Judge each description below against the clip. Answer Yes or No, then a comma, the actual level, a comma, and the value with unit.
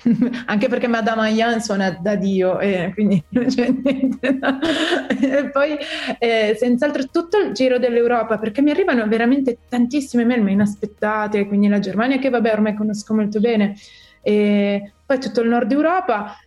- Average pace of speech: Yes, average, 160 wpm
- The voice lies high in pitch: Yes, high, 235 Hz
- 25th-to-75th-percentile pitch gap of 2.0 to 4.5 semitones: Yes, average, 3.8 semitones